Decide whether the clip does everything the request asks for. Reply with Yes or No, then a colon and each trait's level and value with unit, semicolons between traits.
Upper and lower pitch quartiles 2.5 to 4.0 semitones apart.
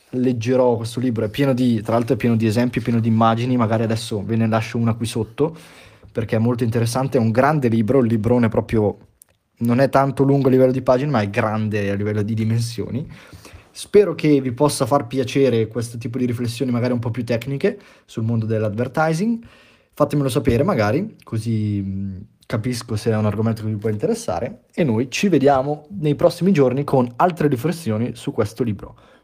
Yes: average, 3.3 semitones